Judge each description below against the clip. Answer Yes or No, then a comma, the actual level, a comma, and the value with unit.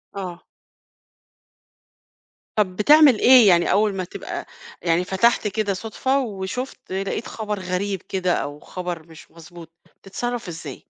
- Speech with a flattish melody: No, average, 3.6 semitones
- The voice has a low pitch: No, high, 195 Hz